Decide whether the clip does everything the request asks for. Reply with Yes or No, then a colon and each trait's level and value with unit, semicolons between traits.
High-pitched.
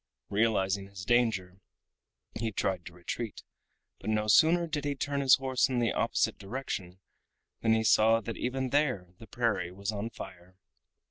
No: low, 110 Hz